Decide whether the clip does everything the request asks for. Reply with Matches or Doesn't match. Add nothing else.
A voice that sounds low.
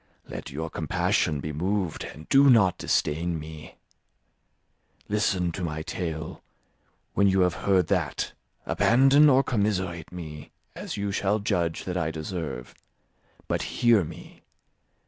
Matches